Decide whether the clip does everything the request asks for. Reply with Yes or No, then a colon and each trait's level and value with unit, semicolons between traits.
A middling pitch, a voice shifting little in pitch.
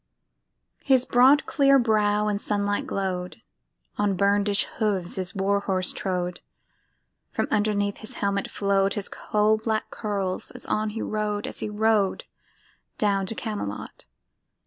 No: high, 205 Hz; narrow, 1.6 semitones